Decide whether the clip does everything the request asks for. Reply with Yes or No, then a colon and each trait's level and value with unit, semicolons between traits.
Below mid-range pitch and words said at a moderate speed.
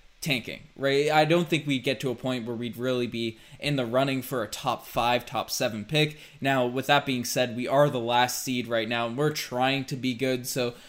No: low, 130 Hz; fast, 235 wpm